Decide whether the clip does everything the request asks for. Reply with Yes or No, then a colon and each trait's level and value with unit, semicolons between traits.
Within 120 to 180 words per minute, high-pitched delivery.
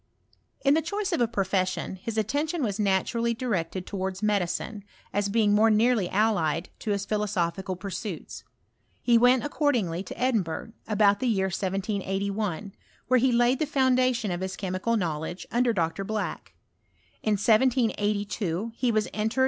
Yes: average, 150 wpm; high, 210 Hz